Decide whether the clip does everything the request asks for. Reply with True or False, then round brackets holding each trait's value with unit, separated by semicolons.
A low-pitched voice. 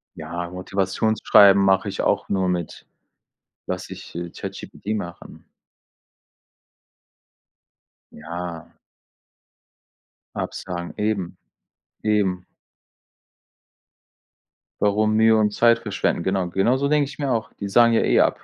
True (100 Hz)